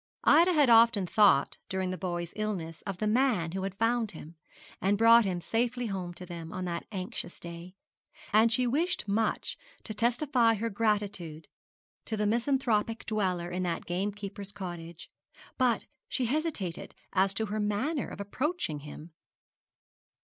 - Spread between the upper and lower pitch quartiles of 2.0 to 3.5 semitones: No, average, 4.3 semitones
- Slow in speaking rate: No, average, 155 wpm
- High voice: Yes, high, 205 Hz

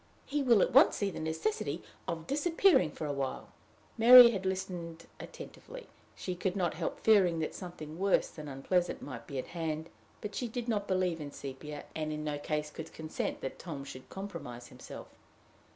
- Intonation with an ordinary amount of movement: Yes, average, 4.7 semitones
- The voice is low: No, medium, 170 Hz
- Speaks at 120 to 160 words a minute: No, average, 185 wpm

